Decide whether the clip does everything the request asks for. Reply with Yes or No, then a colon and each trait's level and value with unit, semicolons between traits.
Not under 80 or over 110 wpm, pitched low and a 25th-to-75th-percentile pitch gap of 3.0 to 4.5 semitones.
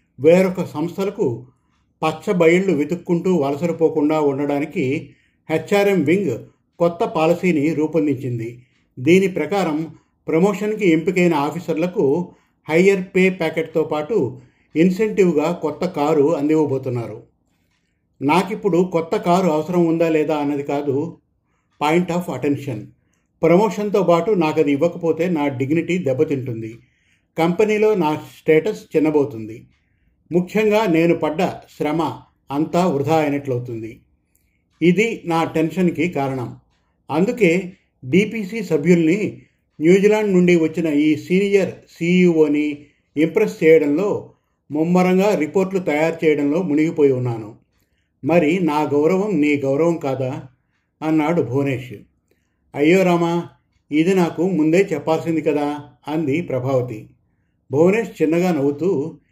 No: average, 95 wpm; medium, 160 Hz; average, 3.4 semitones